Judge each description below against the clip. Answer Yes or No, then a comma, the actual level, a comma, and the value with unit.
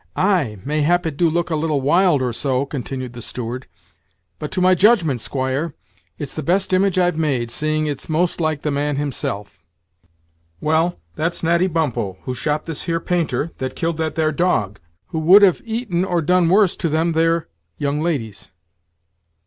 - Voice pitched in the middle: Yes, medium, 155 Hz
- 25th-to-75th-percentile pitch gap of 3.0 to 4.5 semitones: Yes, average, 3.8 semitones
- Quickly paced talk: No, average, 175 wpm